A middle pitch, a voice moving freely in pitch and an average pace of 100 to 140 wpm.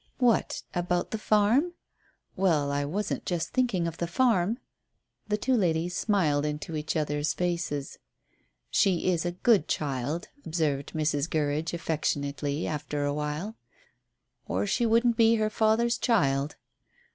Yes: medium, 170 Hz; wide, 6.2 semitones; slow, 135 wpm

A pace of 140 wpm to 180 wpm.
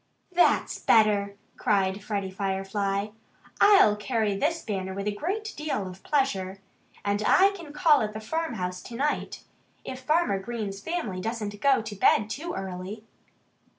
Yes: average, 150 wpm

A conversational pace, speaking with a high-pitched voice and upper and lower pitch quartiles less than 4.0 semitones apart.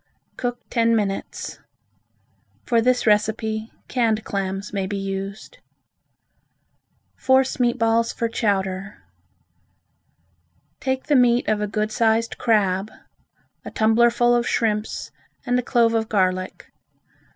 No: slow, 115 wpm; high, 220 Hz; average, 2.8 semitones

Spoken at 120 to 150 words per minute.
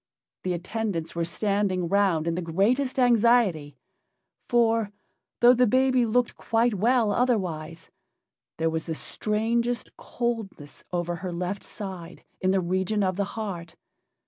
Yes: slow, 135 wpm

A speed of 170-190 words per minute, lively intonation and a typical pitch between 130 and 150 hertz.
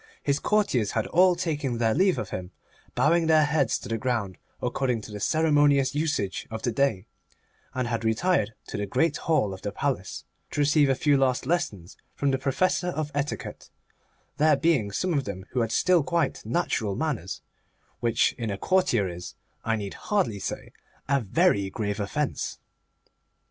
Yes: average, 175 wpm; wide, 6.4 semitones; low, 135 Hz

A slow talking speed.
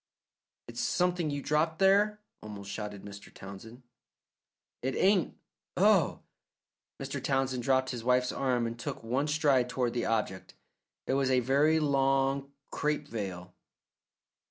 Yes: slow, 130 wpm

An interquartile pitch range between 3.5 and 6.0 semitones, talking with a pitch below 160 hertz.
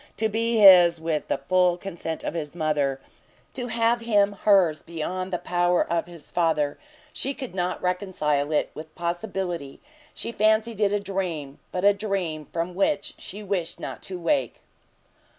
No: average, 3.8 semitones; medium, 180 Hz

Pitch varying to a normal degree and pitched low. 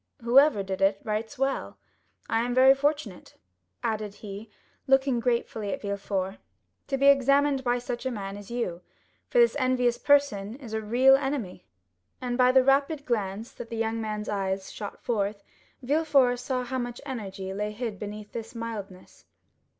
No: average, 4.4 semitones; high, 235 Hz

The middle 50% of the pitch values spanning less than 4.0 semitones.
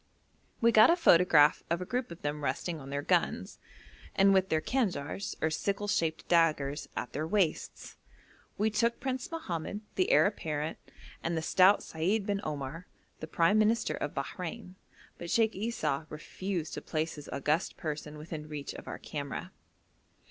No: average, 5.0 semitones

